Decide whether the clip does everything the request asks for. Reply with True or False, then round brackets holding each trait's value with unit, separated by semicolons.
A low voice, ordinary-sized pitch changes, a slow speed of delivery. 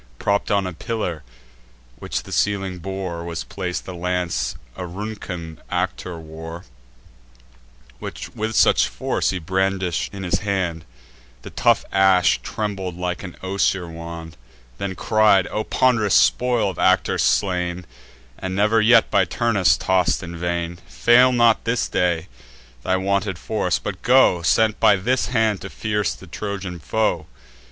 False (95 Hz; 3.2 semitones; 145 wpm)